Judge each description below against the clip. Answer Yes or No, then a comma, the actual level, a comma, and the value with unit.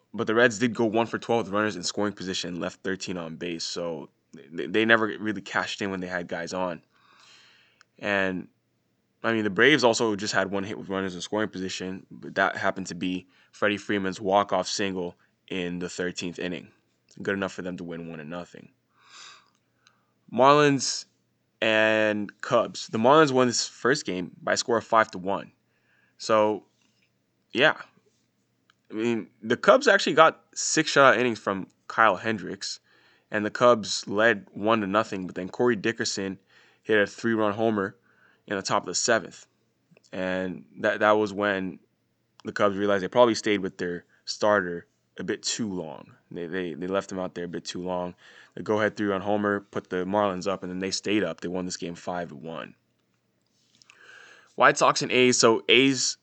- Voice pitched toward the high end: No, low, 100 Hz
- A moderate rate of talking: Yes, average, 185 wpm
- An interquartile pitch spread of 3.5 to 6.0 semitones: No, average, 3.0 semitones